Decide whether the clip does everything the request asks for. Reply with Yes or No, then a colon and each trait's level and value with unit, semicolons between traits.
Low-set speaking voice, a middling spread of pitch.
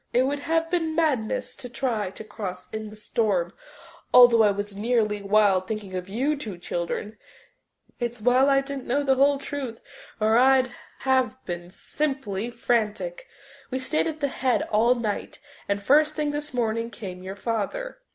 No: high, 235 Hz; average, 4.7 semitones